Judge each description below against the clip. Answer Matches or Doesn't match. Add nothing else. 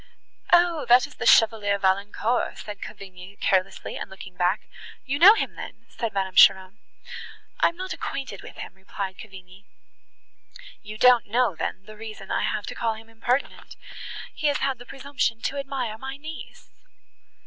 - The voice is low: Doesn't match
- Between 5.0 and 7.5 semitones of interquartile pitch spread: Matches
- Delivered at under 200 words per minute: Matches